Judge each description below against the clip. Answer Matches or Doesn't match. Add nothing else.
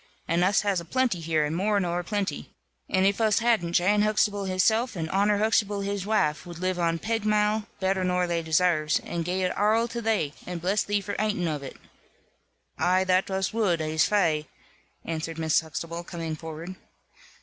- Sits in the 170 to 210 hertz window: Matches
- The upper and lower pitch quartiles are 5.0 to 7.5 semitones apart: Doesn't match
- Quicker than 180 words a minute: Matches